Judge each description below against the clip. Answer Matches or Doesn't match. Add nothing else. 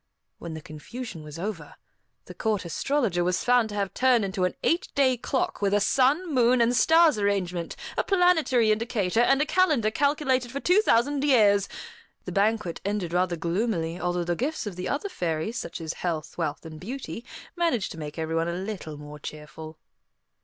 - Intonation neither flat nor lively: Doesn't match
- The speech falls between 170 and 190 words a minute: Matches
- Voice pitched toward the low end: Doesn't match